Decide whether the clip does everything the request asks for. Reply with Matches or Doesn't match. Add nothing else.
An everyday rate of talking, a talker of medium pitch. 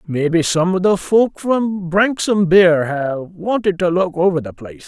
Matches